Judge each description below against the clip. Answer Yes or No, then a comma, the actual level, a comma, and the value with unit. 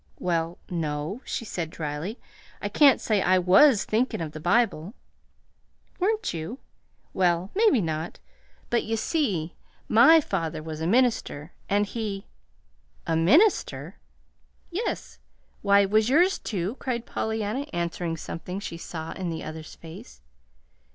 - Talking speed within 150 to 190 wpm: No, slow, 135 wpm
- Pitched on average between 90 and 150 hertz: No, high, 190 Hz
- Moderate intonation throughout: No, wide, 6.4 semitones